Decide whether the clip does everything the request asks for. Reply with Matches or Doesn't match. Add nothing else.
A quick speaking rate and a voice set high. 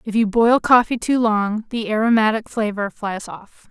Doesn't match